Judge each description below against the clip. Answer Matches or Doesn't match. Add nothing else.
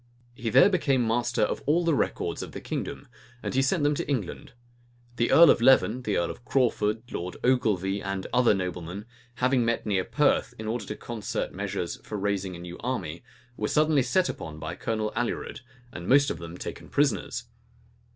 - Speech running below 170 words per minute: Doesn't match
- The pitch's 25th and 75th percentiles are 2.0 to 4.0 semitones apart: Doesn't match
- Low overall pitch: Matches